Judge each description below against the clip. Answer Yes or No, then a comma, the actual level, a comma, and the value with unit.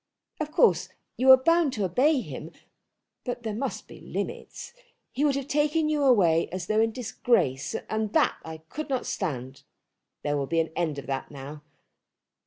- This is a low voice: No, high, 220 Hz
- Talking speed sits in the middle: Yes, average, 180 wpm